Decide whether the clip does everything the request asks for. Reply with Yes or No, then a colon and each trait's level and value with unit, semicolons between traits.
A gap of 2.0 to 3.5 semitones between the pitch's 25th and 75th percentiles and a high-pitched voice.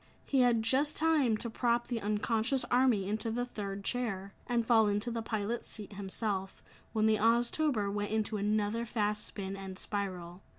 Yes: average, 2.8 semitones; high, 220 Hz